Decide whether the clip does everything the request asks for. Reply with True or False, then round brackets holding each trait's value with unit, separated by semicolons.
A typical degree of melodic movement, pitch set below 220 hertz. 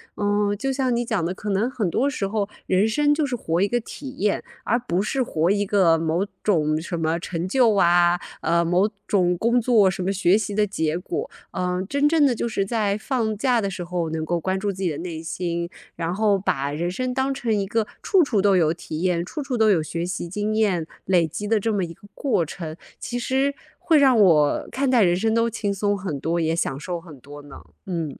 True (4.9 semitones; 195 Hz)